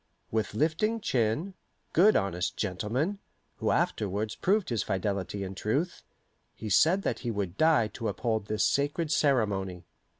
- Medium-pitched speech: No, low, 110 Hz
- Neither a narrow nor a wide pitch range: No, wide, 7.8 semitones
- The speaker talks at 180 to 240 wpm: No, average, 140 wpm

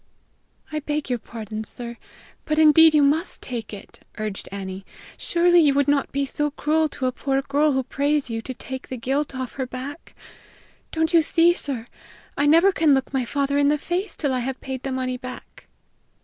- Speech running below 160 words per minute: No, average, 200 wpm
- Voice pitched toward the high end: Yes, very high, 275 Hz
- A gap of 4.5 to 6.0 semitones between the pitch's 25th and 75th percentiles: No, average, 3.0 semitones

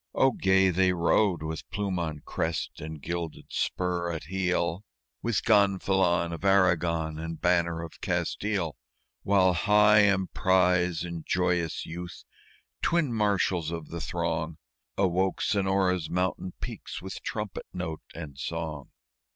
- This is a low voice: Yes, very low, 90 Hz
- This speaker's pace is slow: Yes, slow, 125 wpm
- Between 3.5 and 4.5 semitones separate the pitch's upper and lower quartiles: No, narrow, 2.5 semitones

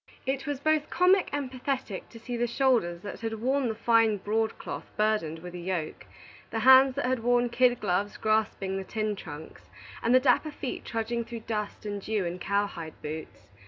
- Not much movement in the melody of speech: No, average, 4.3 semitones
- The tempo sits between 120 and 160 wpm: No, average, 195 wpm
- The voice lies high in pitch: Yes, high, 225 Hz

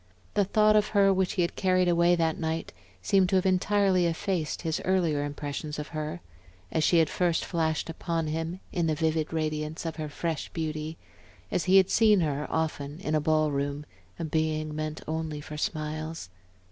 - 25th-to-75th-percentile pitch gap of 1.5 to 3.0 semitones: Yes, average, 2.7 semitones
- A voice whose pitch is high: No, medium, 160 Hz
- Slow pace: No, average, 185 wpm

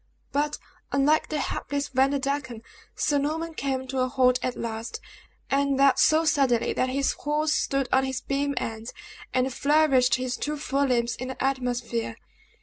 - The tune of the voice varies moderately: No, narrow, 2.1 semitones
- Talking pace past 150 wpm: Yes, average, 160 wpm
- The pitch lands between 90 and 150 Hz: No, very high, 270 Hz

